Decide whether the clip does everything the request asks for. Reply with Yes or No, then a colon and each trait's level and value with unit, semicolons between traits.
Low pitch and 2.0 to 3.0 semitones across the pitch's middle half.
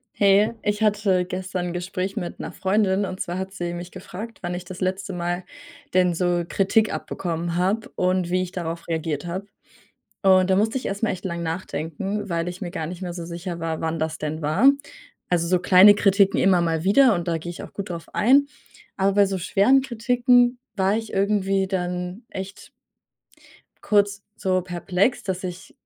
No: medium, 185 Hz; narrow, 2.4 semitones